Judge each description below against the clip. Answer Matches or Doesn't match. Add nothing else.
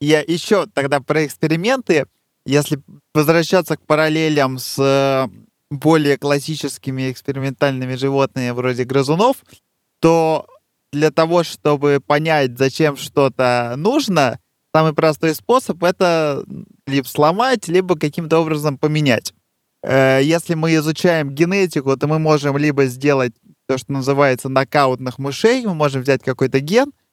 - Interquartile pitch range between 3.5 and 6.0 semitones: Doesn't match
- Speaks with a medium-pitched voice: Matches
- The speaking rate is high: Doesn't match